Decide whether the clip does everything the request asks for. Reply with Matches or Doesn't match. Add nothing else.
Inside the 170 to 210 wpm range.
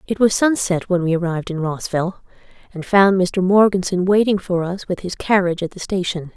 Matches